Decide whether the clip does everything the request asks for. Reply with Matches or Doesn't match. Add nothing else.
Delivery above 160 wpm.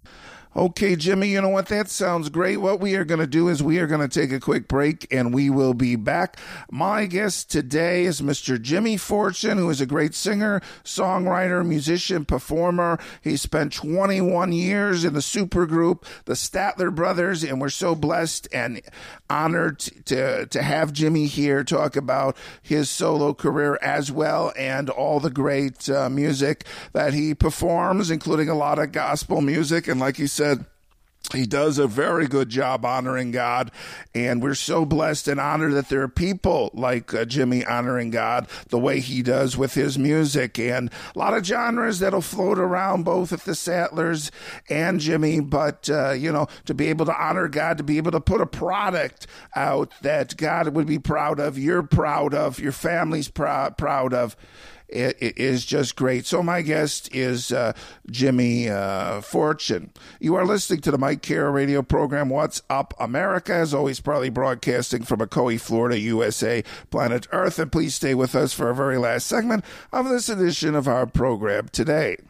Matches